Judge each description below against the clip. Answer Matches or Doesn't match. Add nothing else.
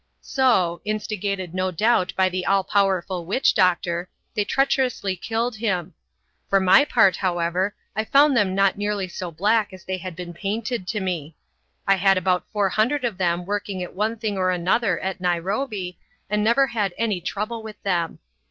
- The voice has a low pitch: Doesn't match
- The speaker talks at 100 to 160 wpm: Doesn't match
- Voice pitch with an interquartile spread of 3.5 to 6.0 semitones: Doesn't match